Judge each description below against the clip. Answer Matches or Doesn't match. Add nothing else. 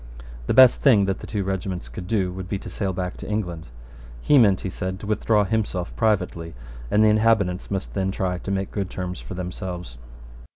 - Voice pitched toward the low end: Matches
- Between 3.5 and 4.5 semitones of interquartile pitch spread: Doesn't match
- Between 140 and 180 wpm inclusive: Doesn't match